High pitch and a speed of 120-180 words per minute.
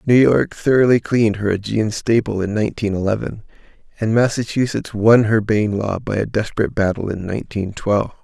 No: low, 110 Hz; average, 170 wpm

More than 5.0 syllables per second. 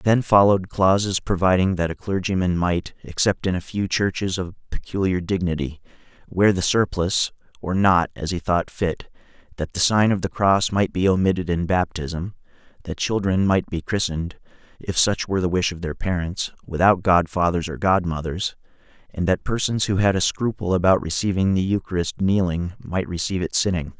Yes: 5.2 syllables/s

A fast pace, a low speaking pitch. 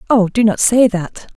No: fast, 215 wpm; high, 215 Hz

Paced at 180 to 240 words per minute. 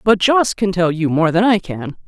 No: fast, 260 wpm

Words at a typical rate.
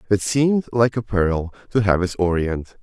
Yes: average, 190 wpm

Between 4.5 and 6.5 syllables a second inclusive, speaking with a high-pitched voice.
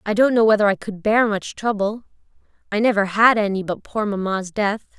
Yes: 5.4 syllables/s; high, 210 Hz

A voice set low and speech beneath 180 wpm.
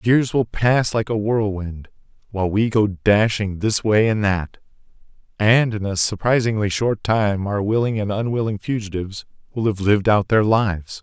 Yes: low, 105 Hz; average, 170 wpm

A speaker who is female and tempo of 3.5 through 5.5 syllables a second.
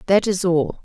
Yes: female; 4.7 syllables/s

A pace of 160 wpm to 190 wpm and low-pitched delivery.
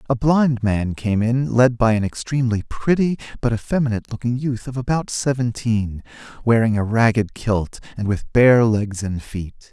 Yes: average, 165 wpm; low, 115 Hz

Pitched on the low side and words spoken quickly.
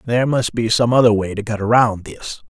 Yes: low, 115 Hz; fast, 240 wpm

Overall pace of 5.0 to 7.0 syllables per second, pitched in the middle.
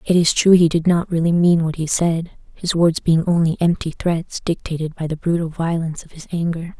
Yes: 5.3 syllables/s; medium, 165 Hz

